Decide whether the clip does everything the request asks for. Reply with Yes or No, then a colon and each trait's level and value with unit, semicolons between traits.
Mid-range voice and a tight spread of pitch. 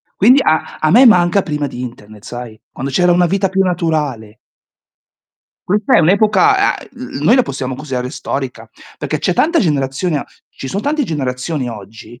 No: medium, 155 Hz; wide, 7.4 semitones